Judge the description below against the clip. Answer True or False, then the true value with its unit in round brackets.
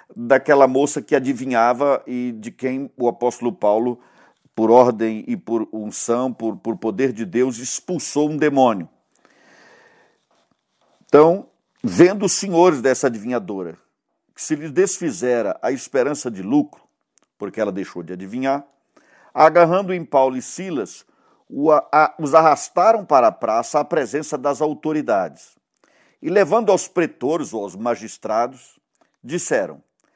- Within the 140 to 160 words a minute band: False (125 wpm)